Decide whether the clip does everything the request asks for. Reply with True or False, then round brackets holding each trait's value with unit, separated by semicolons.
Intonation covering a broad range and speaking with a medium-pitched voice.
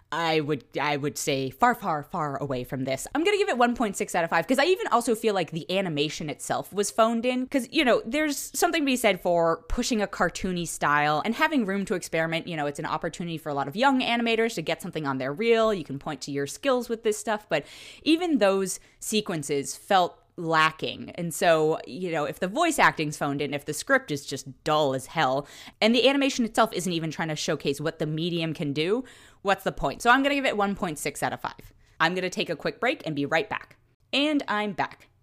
True (7.2 semitones; 175 Hz)